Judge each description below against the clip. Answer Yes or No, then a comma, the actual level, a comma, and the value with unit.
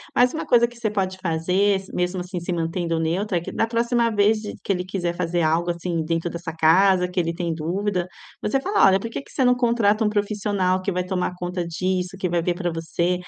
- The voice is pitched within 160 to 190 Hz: Yes, medium, 185 Hz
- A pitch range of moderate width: Yes, average, 3.2 semitones